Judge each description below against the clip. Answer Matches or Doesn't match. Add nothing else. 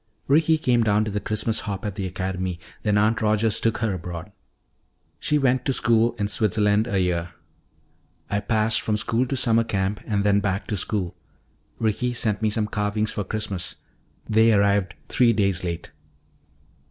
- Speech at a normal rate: Matches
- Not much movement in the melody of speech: Matches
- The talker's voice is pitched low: Matches